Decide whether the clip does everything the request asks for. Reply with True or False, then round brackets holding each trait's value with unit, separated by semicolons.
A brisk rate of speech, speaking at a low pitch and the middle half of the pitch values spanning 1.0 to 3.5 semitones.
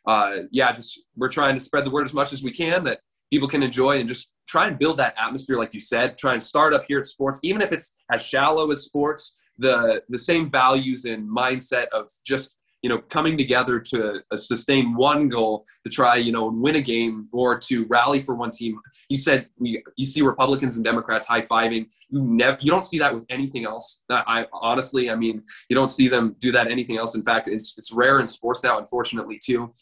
True (230 wpm; 130 Hz; 3.1 semitones)